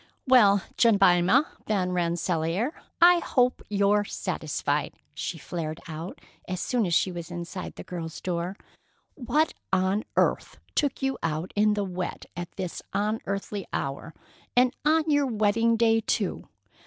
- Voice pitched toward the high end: Yes, high, 200 Hz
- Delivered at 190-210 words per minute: No, average, 140 wpm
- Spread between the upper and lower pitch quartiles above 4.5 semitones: Yes, average, 4.9 semitones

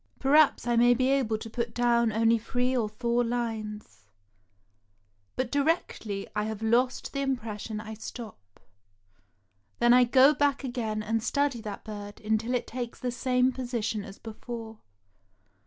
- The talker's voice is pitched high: Yes, high, 235 Hz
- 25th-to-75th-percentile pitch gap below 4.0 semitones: Yes, narrow, 2.5 semitones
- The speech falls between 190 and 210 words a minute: No, average, 155 wpm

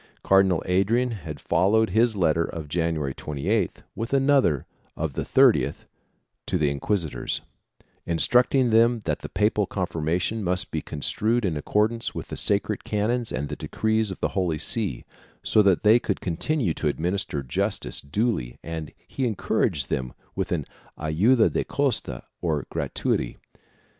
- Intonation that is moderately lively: No, wide, 6.1 semitones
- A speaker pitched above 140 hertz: No, very low, 95 Hz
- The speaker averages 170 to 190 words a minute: No, average, 150 wpm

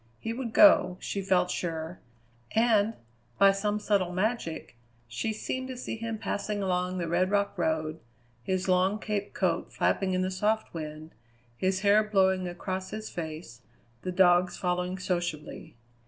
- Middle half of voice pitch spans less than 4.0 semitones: Yes, average, 2.9 semitones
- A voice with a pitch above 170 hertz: Yes, medium, 185 Hz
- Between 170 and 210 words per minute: No, average, 155 wpm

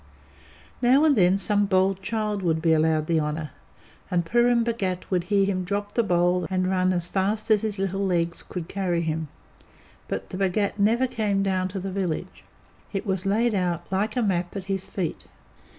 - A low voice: No, high, 190 Hz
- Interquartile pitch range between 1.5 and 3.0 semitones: Yes, narrow, 2.6 semitones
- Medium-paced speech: Yes, average, 190 wpm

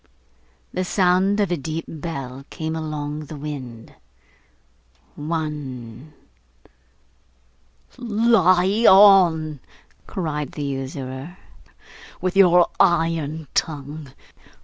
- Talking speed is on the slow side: Yes, slow, 80 wpm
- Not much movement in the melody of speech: No, average, 3.9 semitones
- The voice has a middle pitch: Yes, medium, 160 Hz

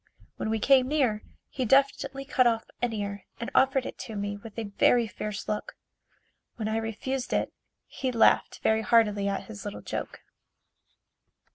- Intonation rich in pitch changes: No, average, 3.5 semitones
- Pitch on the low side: No, high, 225 Hz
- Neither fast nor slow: Yes, average, 165 wpm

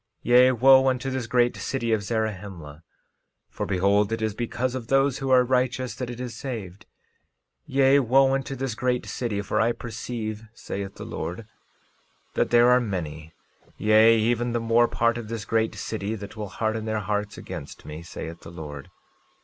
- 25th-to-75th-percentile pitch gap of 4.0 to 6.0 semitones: No, average, 3.4 semitones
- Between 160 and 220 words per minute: Yes, average, 180 wpm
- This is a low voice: Yes, low, 115 Hz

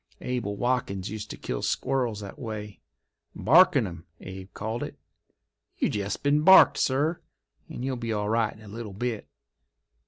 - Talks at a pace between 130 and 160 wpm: Yes, average, 155 wpm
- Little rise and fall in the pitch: No, average, 3.8 semitones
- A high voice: No, low, 110 Hz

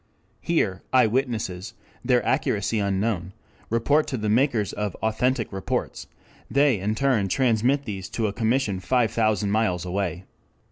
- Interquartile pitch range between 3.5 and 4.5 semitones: Yes, average, 4.1 semitones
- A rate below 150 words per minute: Yes, slow, 135 wpm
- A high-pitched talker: No, low, 110 Hz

